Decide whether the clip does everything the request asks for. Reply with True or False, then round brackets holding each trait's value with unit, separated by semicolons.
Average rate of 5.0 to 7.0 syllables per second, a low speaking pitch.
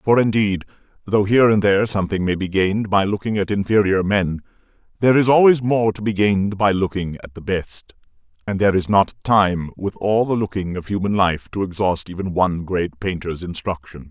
True (5.5 syllables/s; 100 Hz)